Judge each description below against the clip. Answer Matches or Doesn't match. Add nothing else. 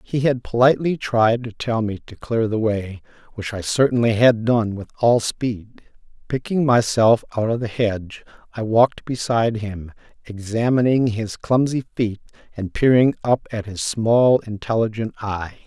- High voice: Doesn't match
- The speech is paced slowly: Doesn't match